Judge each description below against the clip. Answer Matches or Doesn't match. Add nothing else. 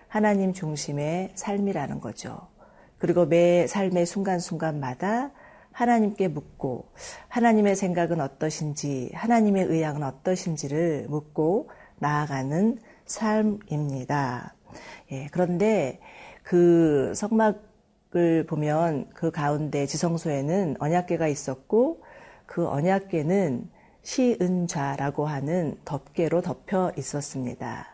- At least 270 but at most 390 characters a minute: Doesn't match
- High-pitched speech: Doesn't match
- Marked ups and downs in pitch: Doesn't match